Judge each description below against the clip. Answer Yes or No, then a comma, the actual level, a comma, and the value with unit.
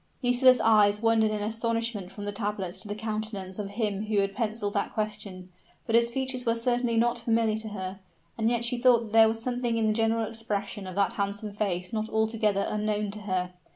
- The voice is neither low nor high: No, high, 215 Hz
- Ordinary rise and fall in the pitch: No, narrow, 2.0 semitones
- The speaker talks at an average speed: No, fast, 210 wpm